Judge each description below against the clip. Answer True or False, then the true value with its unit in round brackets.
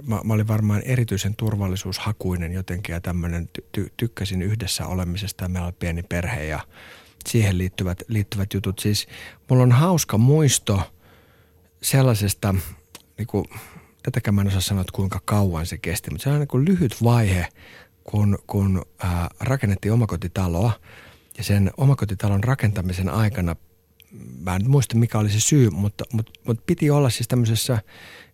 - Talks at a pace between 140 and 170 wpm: True (150 wpm)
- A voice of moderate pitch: False (100 Hz)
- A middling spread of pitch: True (3.8 semitones)